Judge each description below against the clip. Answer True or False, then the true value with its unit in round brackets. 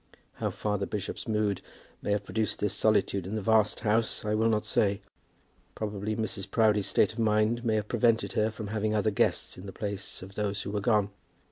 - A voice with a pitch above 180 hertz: False (105 Hz)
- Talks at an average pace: False (210 wpm)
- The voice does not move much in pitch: True (1.3 semitones)